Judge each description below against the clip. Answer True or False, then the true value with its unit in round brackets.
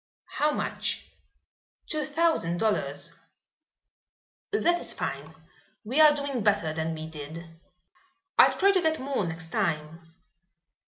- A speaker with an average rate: False (120 wpm)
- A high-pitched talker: True (210 Hz)